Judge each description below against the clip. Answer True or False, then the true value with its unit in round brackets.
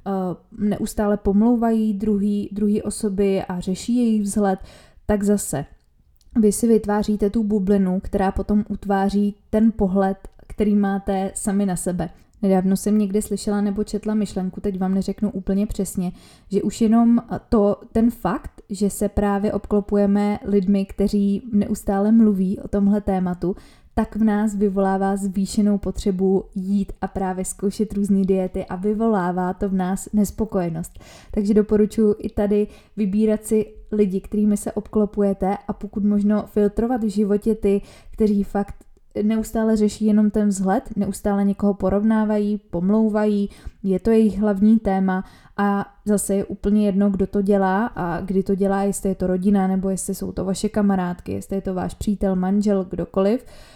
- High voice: True (205 Hz)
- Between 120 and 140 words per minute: False (150 wpm)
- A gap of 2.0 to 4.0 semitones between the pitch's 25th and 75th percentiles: False (1.5 semitones)